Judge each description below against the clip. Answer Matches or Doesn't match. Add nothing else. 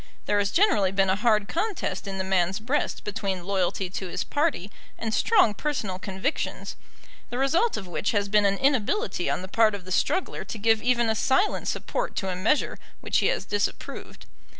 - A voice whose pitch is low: Doesn't match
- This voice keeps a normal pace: Matches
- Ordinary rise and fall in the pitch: Doesn't match